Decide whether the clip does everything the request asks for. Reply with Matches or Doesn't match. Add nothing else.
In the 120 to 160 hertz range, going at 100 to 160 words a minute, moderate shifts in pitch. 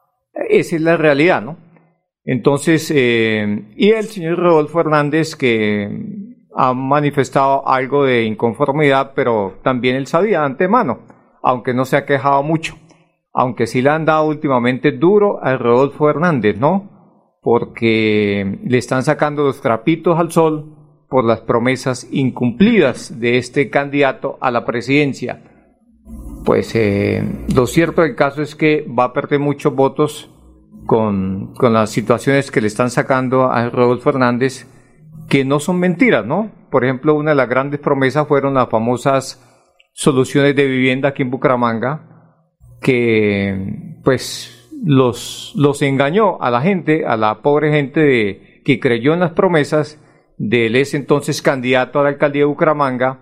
Matches